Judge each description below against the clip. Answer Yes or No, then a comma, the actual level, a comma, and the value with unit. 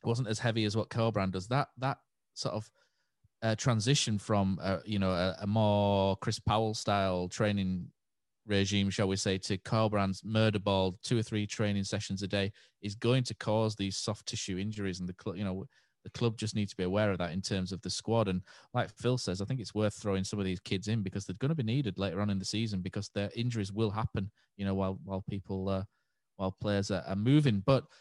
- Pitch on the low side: Yes, low, 105 Hz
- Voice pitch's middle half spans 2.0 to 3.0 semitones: Yes, narrow, 2.4 semitones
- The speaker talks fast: Yes, fast, 235 wpm